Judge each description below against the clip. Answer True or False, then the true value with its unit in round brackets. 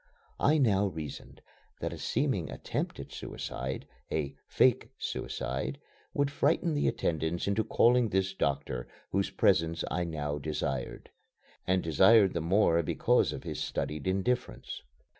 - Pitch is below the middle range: True (85 Hz)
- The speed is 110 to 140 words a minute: True (135 wpm)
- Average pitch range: False (6.2 semitones)